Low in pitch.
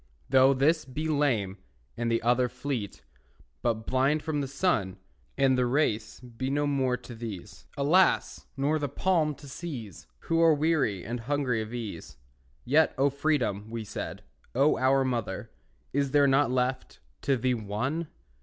Yes: low, 130 Hz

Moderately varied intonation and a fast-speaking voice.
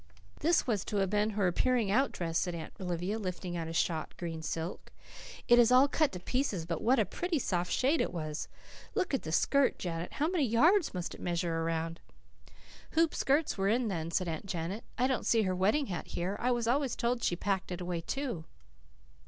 No: wide, 6.7 semitones; fast, 210 wpm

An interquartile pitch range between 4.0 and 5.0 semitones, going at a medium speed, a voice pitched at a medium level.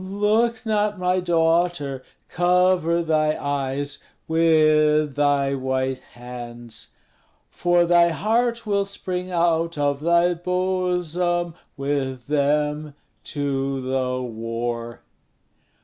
No: average, 4.6 semitones; slow, 95 wpm; medium, 155 Hz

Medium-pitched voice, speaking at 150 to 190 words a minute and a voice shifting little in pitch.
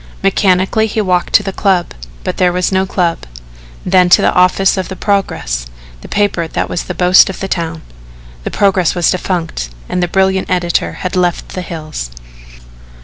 Yes: medium, 180 Hz; average, 185 wpm; narrow, 1.8 semitones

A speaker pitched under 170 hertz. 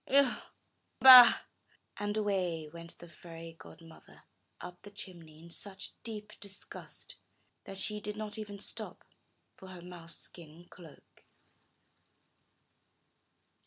No: medium, 185 Hz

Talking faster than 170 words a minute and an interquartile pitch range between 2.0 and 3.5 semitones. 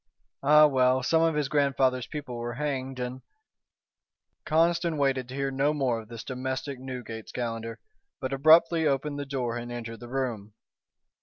No: average, 165 wpm; average, 2.9 semitones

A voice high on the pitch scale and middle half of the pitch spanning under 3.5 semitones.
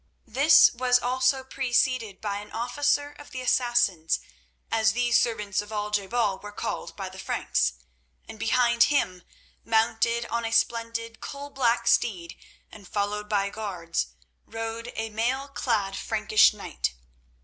Yes: high, 225 Hz; average, 3.0 semitones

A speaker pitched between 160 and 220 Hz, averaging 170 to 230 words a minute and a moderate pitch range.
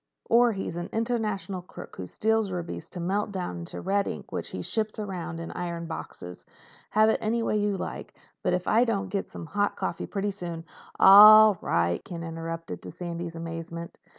Yes: medium, 185 Hz; average, 185 wpm; average, 4.1 semitones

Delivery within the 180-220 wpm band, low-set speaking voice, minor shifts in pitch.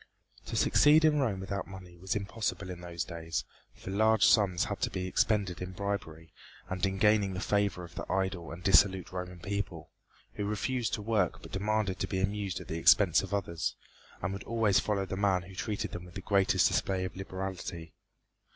Yes: average, 195 wpm; very low, 95 Hz; narrow, 2.1 semitones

